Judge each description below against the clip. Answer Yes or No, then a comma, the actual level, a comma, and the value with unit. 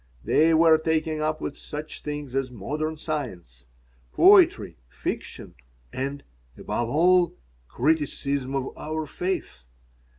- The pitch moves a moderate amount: Yes, average, 3.2 semitones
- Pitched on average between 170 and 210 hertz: No, medium, 150 Hz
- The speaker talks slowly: Yes, slow, 110 wpm